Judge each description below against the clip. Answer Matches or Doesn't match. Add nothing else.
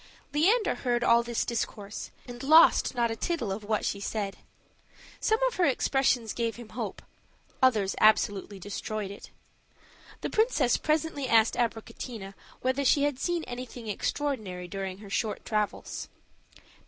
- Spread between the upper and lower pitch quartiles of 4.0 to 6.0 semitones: Matches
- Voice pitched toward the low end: Doesn't match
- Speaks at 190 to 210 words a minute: Doesn't match